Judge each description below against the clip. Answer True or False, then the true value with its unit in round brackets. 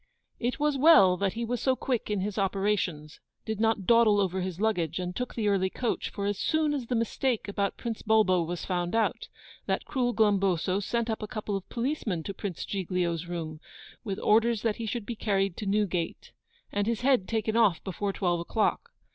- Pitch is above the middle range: True (205 Hz)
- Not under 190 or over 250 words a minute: True (200 wpm)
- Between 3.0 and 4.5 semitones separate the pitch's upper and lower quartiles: True (3.6 semitones)